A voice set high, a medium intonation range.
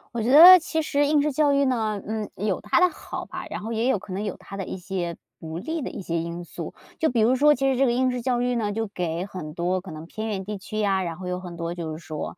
No: high, 210 Hz; wide, 6.2 semitones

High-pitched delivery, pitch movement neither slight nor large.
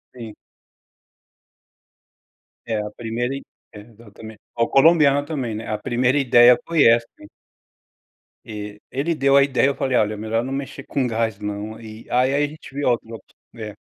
No: low, 120 Hz; average, 3.9 semitones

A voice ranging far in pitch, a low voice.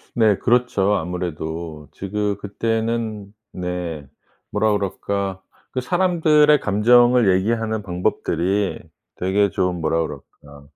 No: average, 4.1 semitones; low, 100 Hz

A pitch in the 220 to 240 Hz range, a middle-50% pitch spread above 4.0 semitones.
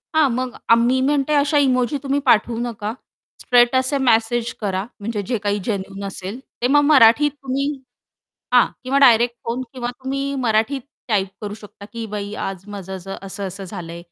Yes: high, 235 Hz; average, 4.4 semitones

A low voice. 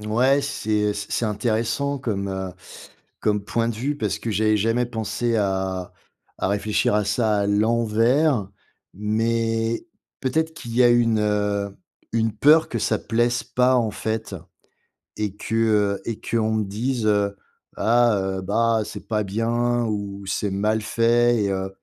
Yes: low, 110 Hz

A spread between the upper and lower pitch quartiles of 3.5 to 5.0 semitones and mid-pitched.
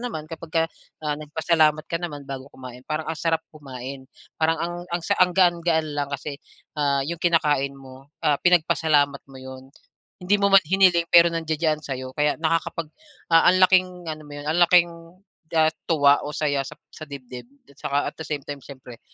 No: average, 3.1 semitones; medium, 155 Hz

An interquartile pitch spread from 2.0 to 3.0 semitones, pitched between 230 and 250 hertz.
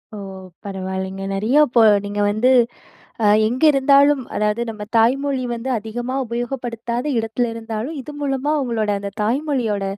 No: average, 3.8 semitones; high, 235 Hz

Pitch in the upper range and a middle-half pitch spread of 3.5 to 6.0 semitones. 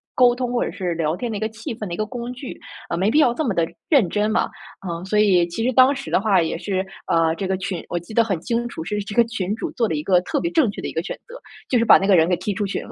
Yes: high, 210 Hz; average, 4.9 semitones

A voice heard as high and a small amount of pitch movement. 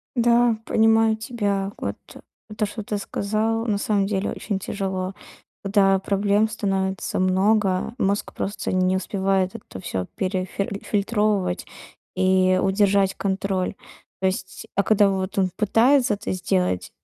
Yes: high, 200 Hz; narrow, 2.0 semitones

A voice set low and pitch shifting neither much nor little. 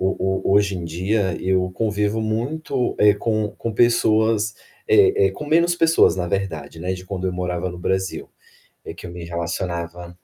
Yes: very low, 95 Hz; average, 3.8 semitones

